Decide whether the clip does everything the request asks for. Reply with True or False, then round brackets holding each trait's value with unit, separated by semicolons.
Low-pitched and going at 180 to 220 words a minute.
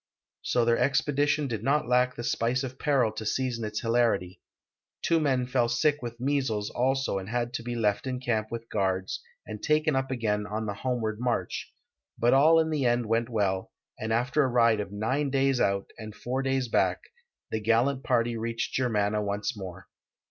True (120 Hz; 190 wpm)